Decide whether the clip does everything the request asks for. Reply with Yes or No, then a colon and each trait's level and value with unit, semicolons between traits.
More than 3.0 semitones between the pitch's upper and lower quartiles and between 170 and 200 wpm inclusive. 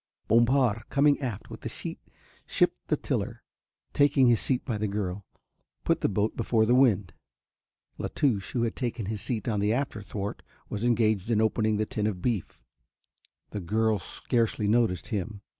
No: average, 2.7 semitones; average, 175 wpm